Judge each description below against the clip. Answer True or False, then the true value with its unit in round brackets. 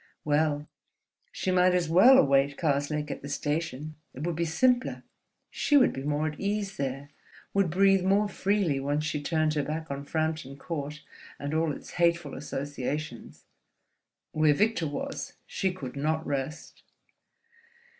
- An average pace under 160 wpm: True (150 wpm)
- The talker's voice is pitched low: False (155 Hz)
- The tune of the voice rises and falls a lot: False (3.8 semitones)